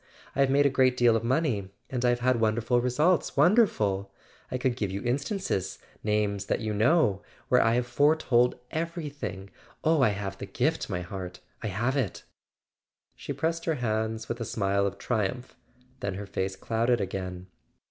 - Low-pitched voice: Yes, low, 120 Hz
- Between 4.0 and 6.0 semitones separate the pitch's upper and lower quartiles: Yes, average, 5.1 semitones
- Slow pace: No, average, 175 wpm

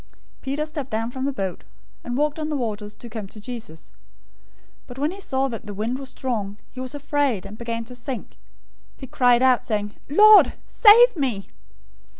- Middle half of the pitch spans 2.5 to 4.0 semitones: No, average, 4.5 semitones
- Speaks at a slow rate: No, average, 190 wpm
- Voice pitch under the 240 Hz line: No, very high, 250 Hz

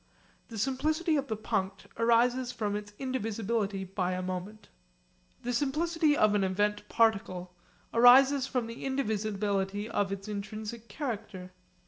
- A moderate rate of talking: No, slow, 130 wpm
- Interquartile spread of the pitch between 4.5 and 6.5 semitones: No, average, 4.0 semitones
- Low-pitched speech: No, high, 220 Hz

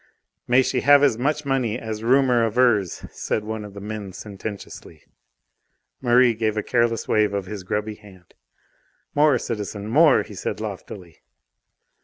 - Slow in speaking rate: No, average, 150 wpm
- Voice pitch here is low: Yes, low, 110 Hz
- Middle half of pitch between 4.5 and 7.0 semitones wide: No, average, 3.5 semitones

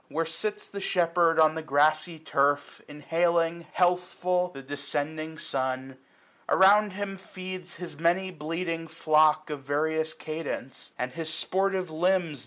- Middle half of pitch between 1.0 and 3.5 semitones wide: Yes, average, 2.9 semitones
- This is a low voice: No, medium, 165 Hz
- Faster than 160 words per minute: No, slow, 135 wpm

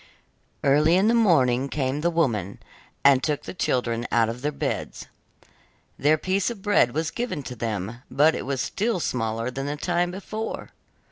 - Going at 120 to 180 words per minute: Yes, average, 175 wpm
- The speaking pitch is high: No, medium, 145 Hz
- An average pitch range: No, wide, 6.1 semitones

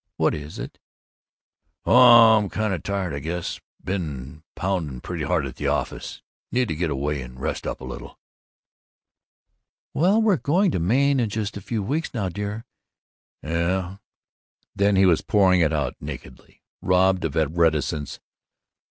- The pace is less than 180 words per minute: Yes, average, 160 wpm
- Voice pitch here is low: Yes, very low, 90 Hz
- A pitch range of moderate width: No, wide, 5.7 semitones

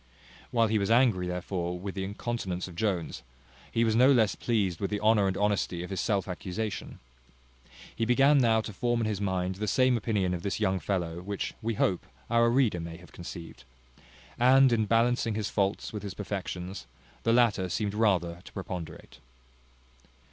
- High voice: No, low, 100 Hz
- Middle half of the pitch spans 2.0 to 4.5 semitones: Yes, average, 3.9 semitones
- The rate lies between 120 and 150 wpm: No, average, 180 wpm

